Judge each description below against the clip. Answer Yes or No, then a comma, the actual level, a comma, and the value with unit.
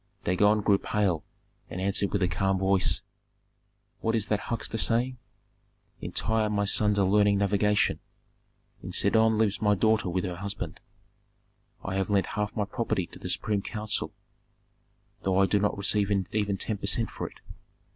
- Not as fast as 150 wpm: No, average, 165 wpm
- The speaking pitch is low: Yes, low, 100 Hz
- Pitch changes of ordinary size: No, narrow, 1.8 semitones